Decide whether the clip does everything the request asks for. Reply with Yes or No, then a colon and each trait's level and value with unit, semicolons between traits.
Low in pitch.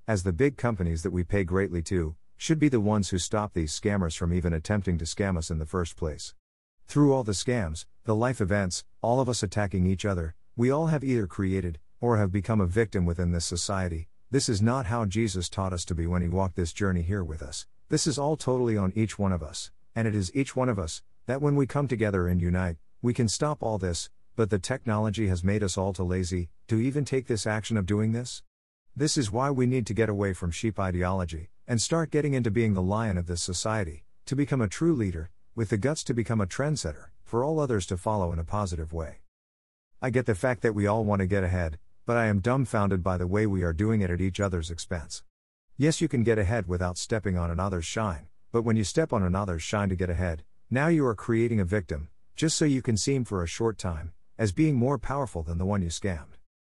Yes: low, 100 Hz